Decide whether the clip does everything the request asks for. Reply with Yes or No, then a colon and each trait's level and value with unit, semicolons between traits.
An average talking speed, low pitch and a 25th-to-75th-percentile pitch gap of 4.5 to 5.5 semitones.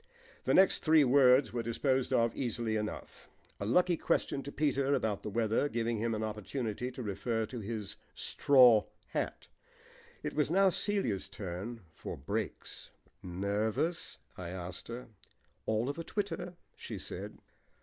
Yes: average, 150 wpm; low, 115 Hz; average, 4.9 semitones